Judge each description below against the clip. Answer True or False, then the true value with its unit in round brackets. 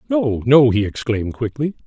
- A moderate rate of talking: True (160 wpm)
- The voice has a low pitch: True (125 Hz)